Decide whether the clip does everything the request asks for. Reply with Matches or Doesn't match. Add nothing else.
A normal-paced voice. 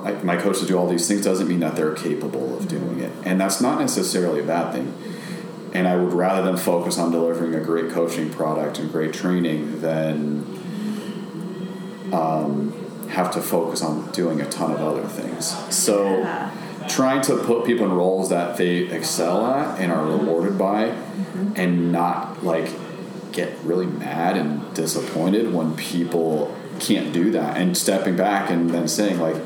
Matches